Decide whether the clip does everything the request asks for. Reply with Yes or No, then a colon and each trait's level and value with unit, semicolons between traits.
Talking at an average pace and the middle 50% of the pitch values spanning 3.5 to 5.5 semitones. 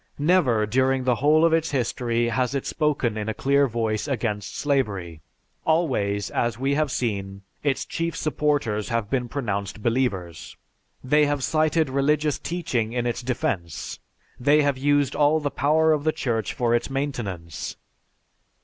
Yes: average, 155 wpm; average, 4.6 semitones